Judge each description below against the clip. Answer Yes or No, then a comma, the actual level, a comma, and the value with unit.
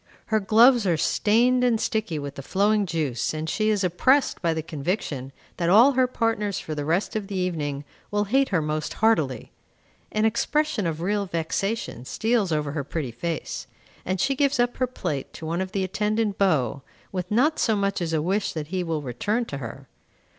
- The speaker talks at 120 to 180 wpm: No, average, 195 wpm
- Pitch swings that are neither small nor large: No, wide, 5.9 semitones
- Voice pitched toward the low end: No, high, 190 Hz